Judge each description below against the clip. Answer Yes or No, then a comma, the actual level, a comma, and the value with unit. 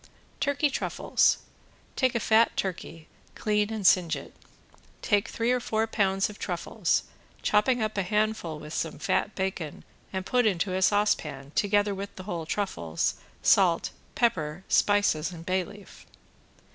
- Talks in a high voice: Yes, high, 200 Hz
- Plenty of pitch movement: No, average, 3.7 semitones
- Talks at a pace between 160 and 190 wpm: No, average, 150 wpm